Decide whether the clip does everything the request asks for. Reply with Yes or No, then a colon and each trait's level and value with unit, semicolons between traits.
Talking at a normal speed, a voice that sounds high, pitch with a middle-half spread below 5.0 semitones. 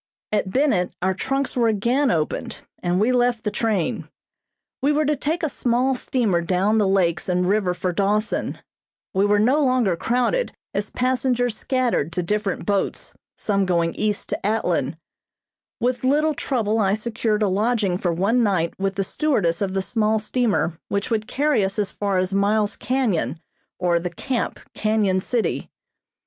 Yes: average, 165 wpm; high, 210 Hz; average, 4.5 semitones